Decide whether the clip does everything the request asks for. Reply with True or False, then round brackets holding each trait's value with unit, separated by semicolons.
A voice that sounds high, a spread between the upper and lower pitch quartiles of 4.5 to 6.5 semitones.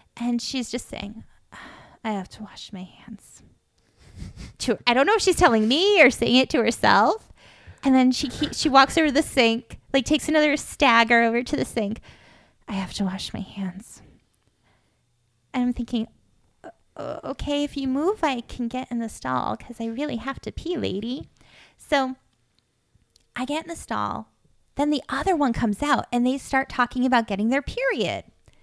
True (245 Hz; 5.2 semitones)